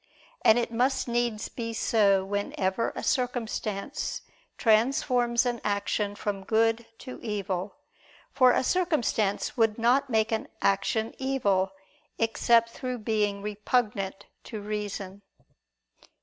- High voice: Yes, high, 225 Hz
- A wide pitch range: No, average, 3.0 semitones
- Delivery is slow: Yes, slow, 115 wpm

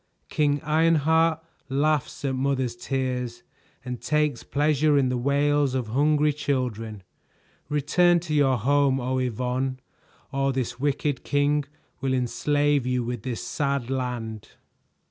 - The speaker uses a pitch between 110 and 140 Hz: Yes, low, 135 Hz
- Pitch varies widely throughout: No, average, 2.7 semitones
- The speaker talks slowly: Yes, slow, 125 wpm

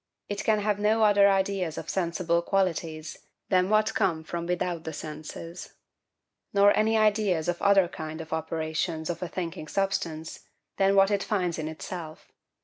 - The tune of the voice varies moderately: Yes, average, 3.7 semitones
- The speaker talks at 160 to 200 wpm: Yes, average, 170 wpm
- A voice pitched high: No, medium, 180 Hz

